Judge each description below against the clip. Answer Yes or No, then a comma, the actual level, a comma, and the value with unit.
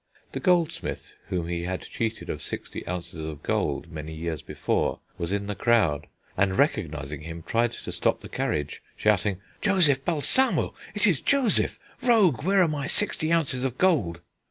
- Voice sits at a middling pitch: No, low, 115 Hz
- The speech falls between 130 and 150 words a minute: No, average, 165 wpm